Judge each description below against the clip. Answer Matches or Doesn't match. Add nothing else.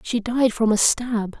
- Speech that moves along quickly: Matches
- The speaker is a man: Doesn't match